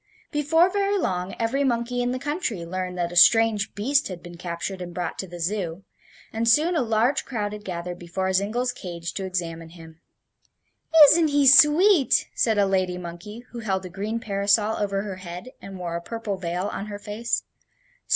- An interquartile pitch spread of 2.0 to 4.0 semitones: No, average, 5.1 semitones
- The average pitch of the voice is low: No, high, 205 Hz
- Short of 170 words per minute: No, average, 190 wpm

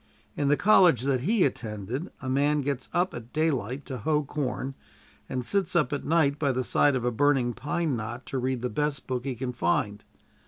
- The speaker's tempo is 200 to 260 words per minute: Yes, fast, 205 wpm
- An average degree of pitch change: Yes, average, 3.1 semitones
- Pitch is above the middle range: No, low, 135 Hz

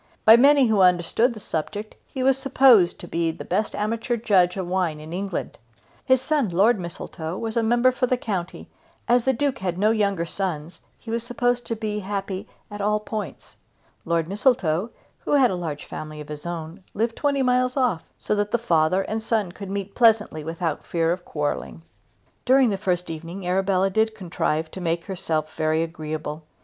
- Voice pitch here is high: Yes, high, 195 Hz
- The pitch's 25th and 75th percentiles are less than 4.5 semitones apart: No, average, 5.3 semitones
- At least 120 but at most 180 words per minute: No, average, 190 wpm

